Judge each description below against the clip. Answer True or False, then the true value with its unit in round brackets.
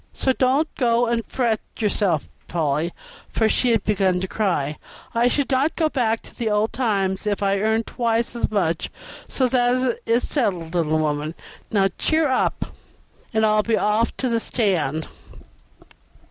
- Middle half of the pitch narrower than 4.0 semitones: False (4.3 semitones)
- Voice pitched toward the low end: False (220 Hz)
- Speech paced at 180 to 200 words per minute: False (160 wpm)